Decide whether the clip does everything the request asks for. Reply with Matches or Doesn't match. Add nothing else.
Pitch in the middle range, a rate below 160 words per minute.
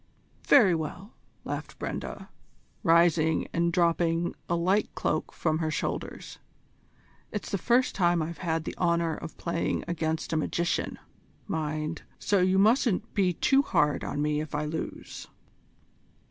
Matches